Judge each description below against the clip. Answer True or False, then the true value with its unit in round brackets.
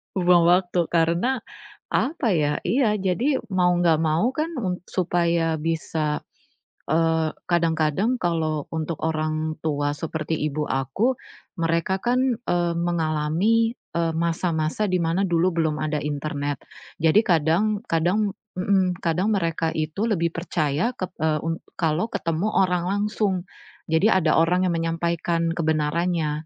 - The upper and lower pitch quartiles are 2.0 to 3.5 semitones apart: True (2.9 semitones)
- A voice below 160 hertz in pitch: False (170 Hz)